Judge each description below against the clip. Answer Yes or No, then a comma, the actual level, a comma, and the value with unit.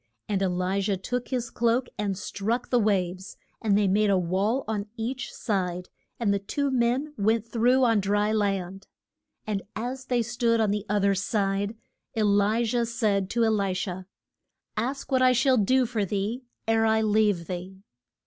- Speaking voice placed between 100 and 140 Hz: No, high, 215 Hz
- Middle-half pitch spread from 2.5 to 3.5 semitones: Yes, average, 3.2 semitones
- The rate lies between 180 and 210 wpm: Yes, average, 185 wpm